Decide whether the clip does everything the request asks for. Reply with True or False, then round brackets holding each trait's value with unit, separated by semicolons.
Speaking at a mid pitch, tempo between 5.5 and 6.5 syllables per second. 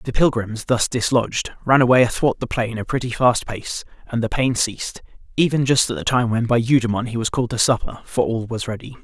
False (120 Hz; 5.7 syllables/s)